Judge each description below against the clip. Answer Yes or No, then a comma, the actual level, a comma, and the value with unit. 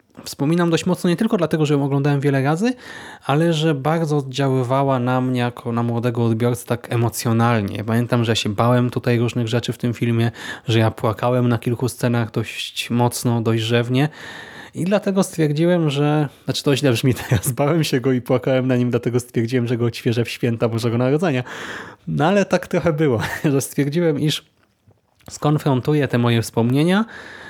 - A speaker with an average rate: No, fast, 175 wpm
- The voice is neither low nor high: No, low, 130 Hz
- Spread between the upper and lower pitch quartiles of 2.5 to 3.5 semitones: No, average, 4.1 semitones